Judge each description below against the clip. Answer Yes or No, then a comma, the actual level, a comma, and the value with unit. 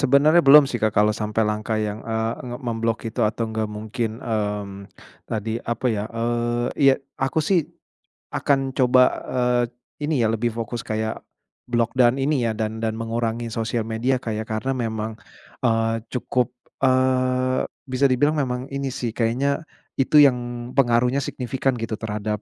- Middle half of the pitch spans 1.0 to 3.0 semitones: Yes, average, 2.7 semitones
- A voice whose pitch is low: Yes, low, 120 Hz